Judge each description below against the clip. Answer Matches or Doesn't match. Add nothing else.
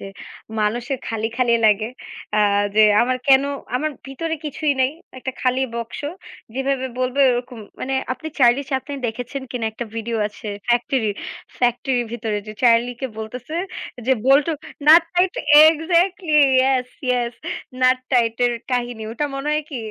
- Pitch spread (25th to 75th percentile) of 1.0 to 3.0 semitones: Matches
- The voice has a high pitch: Matches